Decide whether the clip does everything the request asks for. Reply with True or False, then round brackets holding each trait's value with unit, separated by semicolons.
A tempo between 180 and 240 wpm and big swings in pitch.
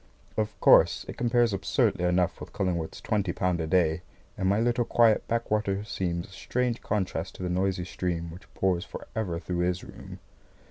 False (185 wpm; 3.3 semitones)